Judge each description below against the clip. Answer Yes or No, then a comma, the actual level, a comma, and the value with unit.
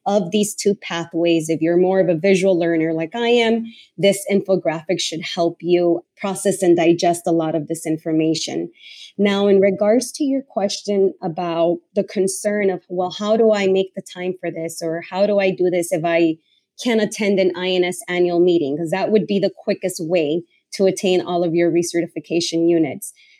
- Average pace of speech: Yes, average, 190 wpm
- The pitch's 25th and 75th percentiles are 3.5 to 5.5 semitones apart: No, average, 2.9 semitones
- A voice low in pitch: No, medium, 185 Hz